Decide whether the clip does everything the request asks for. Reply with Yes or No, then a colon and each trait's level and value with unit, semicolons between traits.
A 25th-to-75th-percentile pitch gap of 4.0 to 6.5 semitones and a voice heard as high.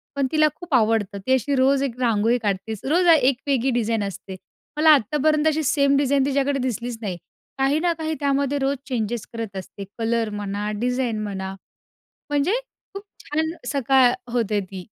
Yes: average, 4.4 semitones; very high, 255 Hz